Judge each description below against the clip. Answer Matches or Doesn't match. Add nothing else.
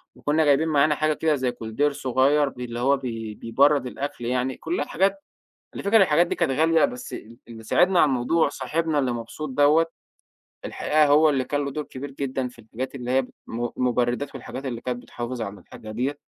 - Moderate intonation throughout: Matches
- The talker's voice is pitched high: Doesn't match